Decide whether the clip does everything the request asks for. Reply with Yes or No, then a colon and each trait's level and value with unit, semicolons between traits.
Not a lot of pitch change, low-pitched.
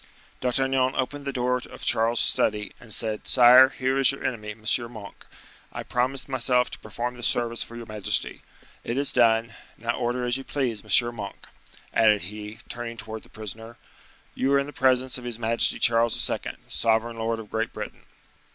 Yes: narrow, 2.2 semitones; low, 120 Hz